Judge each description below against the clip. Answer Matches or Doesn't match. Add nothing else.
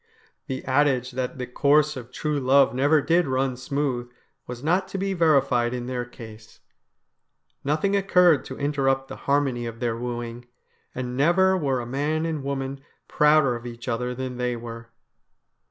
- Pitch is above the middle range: Doesn't match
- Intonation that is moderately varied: Matches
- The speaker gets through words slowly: Doesn't match